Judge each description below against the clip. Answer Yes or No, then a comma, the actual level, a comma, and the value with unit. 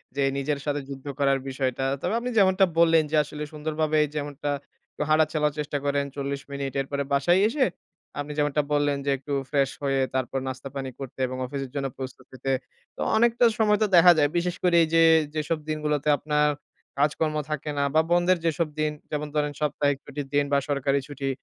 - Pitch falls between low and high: Yes, medium, 145 Hz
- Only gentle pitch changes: Yes, narrow, 2.0 semitones